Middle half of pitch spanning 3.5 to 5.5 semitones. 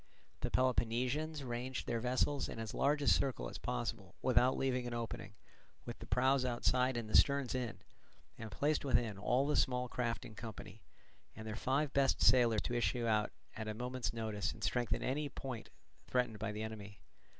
No: average, 2.9 semitones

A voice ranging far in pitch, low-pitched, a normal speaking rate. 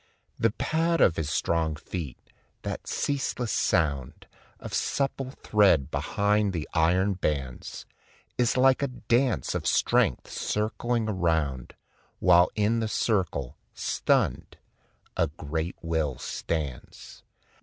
No: wide, 6.5 semitones; very low, 90 Hz; slow, 110 wpm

